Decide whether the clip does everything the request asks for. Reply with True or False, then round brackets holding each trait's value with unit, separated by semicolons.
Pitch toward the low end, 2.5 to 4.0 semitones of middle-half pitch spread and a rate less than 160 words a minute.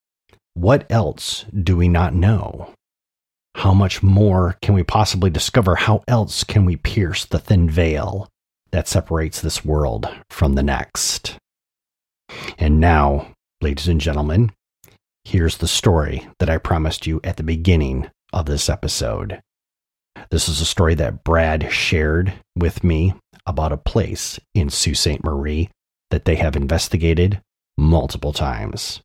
True (85 Hz; 3.7 semitones; 140 wpm)